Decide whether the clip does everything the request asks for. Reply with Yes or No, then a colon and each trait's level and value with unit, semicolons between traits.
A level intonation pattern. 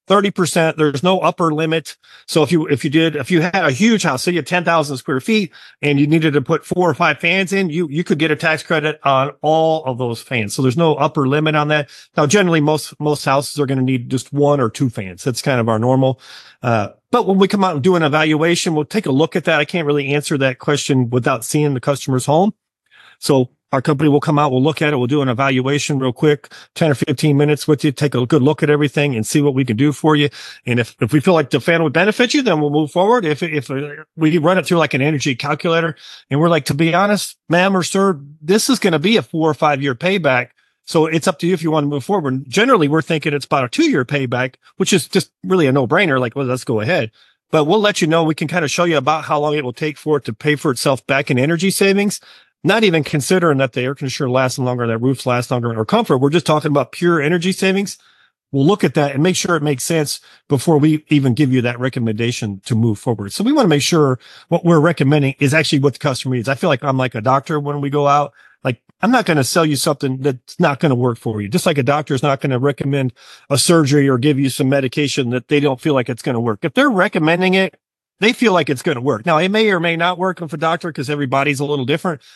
No: average, 3.6 semitones